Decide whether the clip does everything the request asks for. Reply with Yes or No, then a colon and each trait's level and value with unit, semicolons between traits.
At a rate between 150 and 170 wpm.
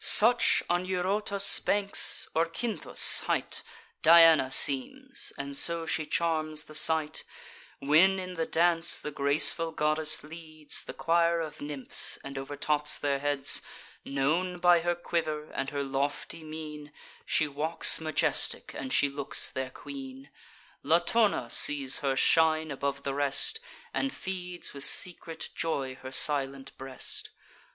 No: slow, 135 wpm